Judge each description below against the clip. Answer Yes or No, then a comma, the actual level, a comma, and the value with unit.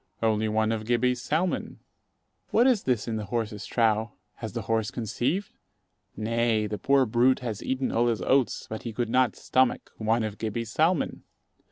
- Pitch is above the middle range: No, low, 115 Hz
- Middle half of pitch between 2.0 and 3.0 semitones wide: Yes, narrow, 2.6 semitones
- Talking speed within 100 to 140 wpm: No, average, 175 wpm